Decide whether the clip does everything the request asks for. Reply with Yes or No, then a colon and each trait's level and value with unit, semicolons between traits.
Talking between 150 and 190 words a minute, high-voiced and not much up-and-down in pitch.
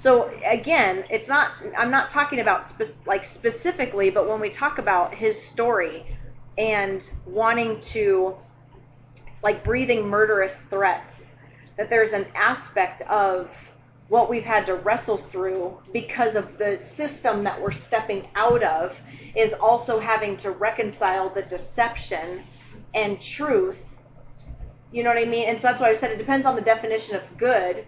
No: average, 155 wpm; high, 215 Hz; average, 3.7 semitones